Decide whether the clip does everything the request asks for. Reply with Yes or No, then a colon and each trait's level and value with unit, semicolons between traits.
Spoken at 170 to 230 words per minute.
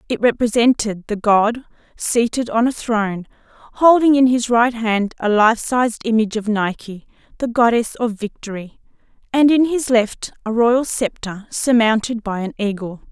No: average, 155 wpm